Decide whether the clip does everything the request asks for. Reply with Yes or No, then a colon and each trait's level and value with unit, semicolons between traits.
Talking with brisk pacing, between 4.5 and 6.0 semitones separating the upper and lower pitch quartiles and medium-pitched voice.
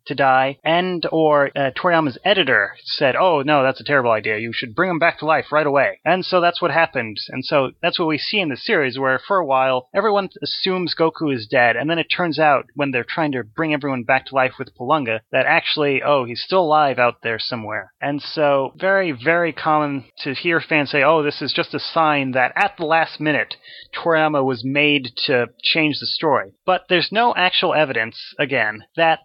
No: fast, 215 wpm; average, 3.9 semitones; medium, 145 Hz